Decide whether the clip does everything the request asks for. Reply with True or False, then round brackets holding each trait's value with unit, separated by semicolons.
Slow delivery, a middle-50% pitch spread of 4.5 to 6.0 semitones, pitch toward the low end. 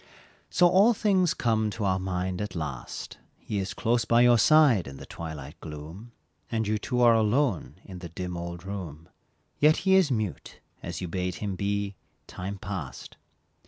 False (175 wpm; 5.1 semitones; 100 Hz)